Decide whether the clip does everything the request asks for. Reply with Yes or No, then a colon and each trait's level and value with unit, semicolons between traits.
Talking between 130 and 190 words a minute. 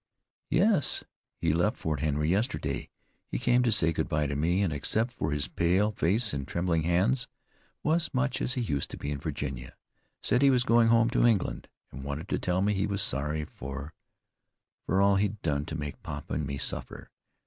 No: average, 200 wpm